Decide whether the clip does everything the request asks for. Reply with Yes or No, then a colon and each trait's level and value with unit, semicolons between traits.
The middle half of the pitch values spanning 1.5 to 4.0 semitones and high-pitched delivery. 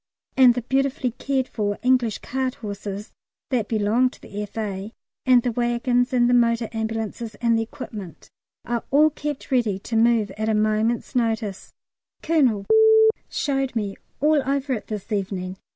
Yes: average, 3.2 semitones; high, 230 Hz